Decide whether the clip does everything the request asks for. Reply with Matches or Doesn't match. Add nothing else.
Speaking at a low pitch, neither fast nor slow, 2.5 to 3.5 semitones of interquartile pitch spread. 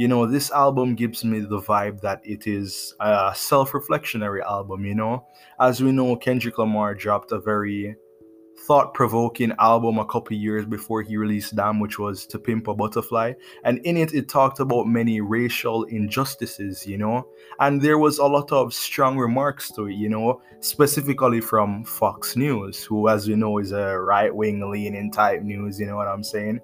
Matches